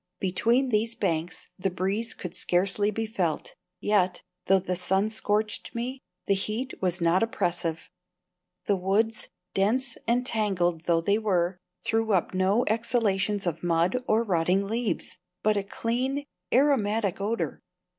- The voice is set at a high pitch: Yes, high, 200 Hz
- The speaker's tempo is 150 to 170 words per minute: No, average, 140 wpm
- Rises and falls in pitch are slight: No, average, 3.8 semitones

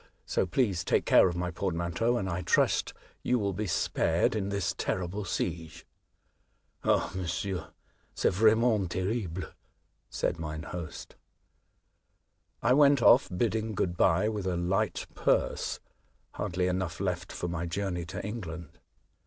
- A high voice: No, very low, 95 Hz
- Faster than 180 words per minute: No, average, 145 wpm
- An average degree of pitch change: Yes, average, 3.4 semitones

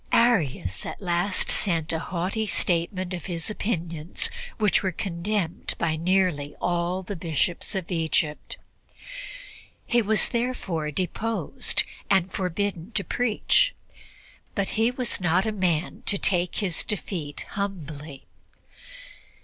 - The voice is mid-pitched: Yes, medium, 180 Hz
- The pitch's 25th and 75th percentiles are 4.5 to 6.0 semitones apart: No, average, 3.6 semitones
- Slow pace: Yes, slow, 120 wpm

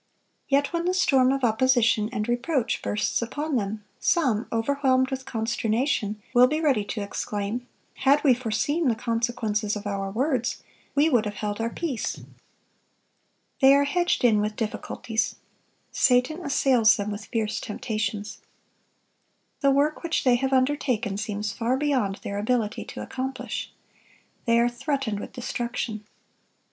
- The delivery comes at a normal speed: Yes, average, 145 wpm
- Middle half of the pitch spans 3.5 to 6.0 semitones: Yes, average, 4.1 semitones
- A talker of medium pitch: No, high, 240 Hz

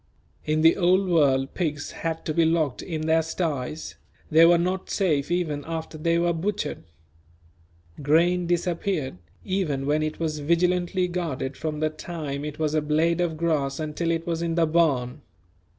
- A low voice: No, medium, 160 Hz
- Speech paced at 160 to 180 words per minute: Yes, average, 165 wpm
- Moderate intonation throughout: No, narrow, 2.3 semitones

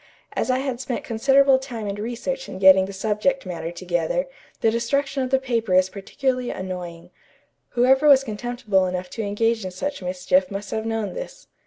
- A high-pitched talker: Yes, high, 225 Hz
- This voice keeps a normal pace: Yes, average, 180 wpm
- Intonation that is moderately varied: No, wide, 5.8 semitones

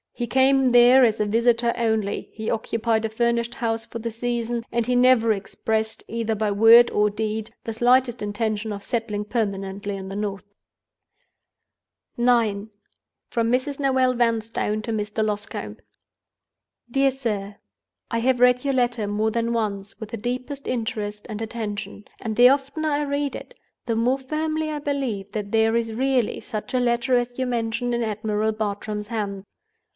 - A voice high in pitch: Yes, high, 230 Hz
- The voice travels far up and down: No, narrow, 2.6 semitones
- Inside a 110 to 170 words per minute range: Yes, average, 165 wpm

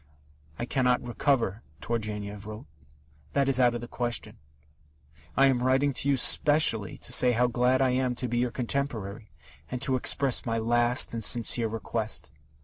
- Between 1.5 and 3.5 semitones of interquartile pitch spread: Yes, narrow, 2.4 semitones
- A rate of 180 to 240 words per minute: No, average, 165 wpm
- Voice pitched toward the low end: Yes, low, 120 Hz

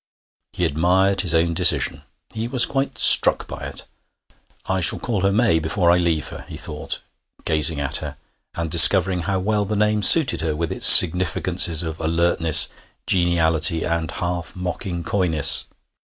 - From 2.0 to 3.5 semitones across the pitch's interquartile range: Yes, average, 2.9 semitones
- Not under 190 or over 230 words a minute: No, average, 160 wpm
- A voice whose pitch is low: Yes, very low, 85 Hz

